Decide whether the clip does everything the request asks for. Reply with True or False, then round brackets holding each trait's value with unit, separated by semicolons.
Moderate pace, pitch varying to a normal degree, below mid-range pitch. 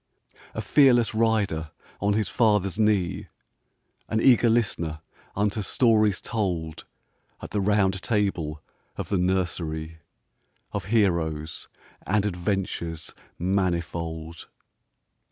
False (100 wpm; 4.2 semitones; 95 Hz)